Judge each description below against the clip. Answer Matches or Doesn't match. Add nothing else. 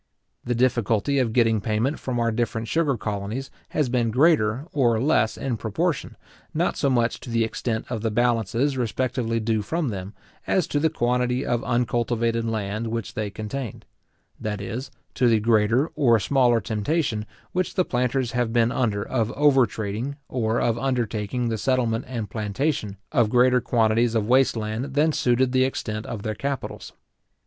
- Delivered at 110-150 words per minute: Doesn't match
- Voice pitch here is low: Matches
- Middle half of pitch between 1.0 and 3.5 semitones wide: Matches